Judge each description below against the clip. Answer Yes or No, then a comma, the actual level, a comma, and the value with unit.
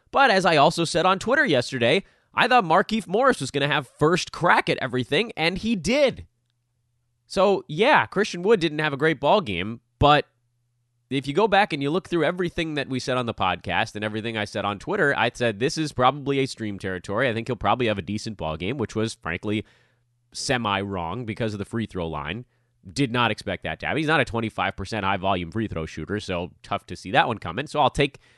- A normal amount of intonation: No, wide, 5.8 semitones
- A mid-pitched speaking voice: No, low, 120 Hz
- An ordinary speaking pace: No, fast, 230 wpm